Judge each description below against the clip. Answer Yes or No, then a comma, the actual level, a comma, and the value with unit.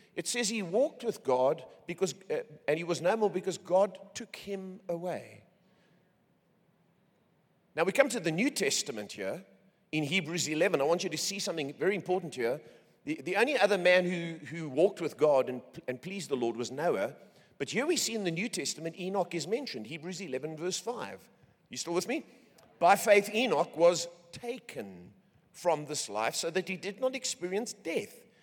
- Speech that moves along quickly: No, average, 190 wpm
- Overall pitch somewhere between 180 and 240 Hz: Yes, medium, 185 Hz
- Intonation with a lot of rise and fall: No, average, 3.9 semitones